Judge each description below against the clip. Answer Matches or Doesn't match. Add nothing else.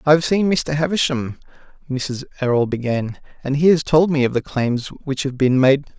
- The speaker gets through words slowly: Doesn't match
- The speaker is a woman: Doesn't match